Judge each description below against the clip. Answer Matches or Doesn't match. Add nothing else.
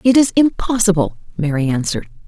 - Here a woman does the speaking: Matches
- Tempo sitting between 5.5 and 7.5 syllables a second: Matches